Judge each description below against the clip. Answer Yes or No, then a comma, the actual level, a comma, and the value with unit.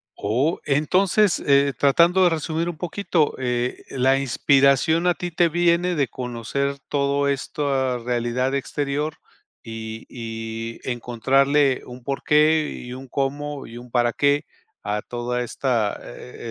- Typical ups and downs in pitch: Yes, average, 3.6 semitones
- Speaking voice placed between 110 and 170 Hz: Yes, medium, 140 Hz